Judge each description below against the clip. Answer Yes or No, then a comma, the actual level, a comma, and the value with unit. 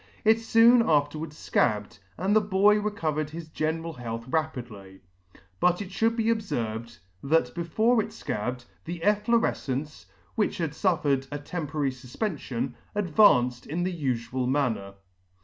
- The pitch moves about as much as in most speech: No, wide, 8.0 semitones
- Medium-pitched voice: Yes, medium, 155 Hz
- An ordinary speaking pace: No, slow, 130 wpm